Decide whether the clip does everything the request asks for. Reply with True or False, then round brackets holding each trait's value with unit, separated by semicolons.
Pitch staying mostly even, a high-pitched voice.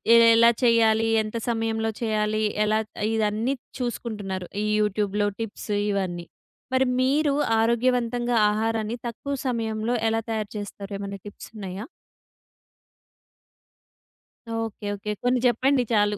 True (2.1 semitones; 220 Hz)